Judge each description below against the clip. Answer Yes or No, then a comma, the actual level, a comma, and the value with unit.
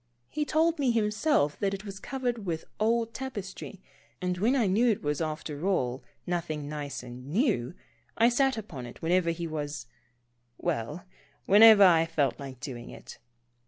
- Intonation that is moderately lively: No, wide, 7.3 semitones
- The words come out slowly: No, average, 170 wpm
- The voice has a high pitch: No, medium, 180 Hz